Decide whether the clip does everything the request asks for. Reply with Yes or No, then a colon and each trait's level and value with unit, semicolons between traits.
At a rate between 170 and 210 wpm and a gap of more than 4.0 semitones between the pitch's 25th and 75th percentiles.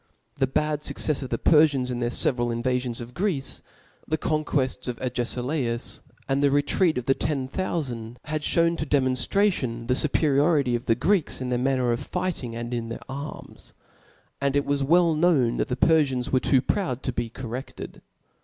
No: average, 180 wpm; average, 3.7 semitones